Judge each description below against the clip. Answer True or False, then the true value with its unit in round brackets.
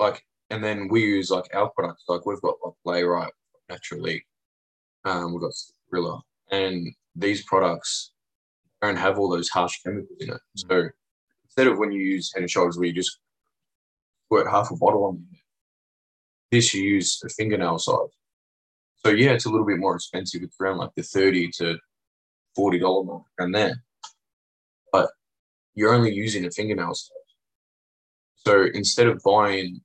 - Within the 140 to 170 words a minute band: True (165 wpm)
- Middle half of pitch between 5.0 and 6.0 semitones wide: False (3.6 semitones)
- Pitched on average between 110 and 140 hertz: False (95 Hz)